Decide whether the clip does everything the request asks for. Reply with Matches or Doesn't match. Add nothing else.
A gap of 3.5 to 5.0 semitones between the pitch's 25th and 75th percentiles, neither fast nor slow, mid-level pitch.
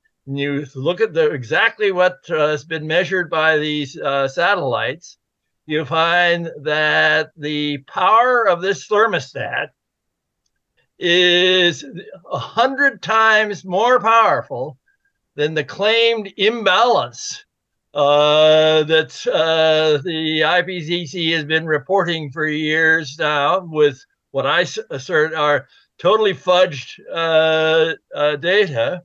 Doesn't match